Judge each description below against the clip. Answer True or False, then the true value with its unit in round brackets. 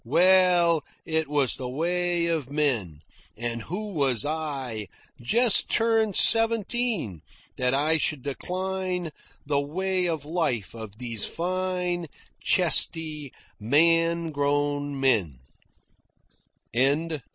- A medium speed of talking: False (100 wpm)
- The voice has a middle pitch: True (155 Hz)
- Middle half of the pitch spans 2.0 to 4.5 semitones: False (5.2 semitones)